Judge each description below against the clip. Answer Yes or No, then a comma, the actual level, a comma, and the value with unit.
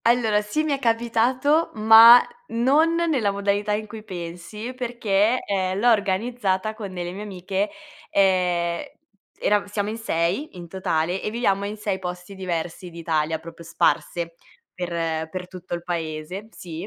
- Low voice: No, high, 195 Hz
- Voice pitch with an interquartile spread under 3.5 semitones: No, average, 4.2 semitones